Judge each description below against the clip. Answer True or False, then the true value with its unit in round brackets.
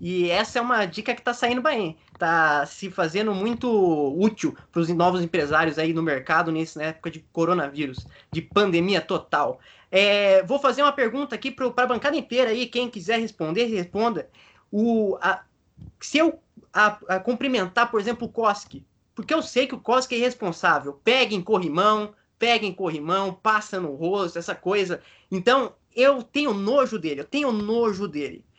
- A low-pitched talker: False (210 Hz)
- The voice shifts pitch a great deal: True (5.9 semitones)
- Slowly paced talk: False (170 wpm)